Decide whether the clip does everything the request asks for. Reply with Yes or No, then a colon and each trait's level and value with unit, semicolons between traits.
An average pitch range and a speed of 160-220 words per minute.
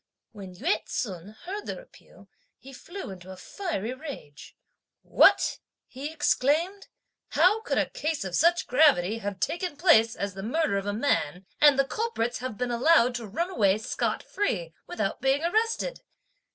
No: wide, 8.7 semitones; average, 165 wpm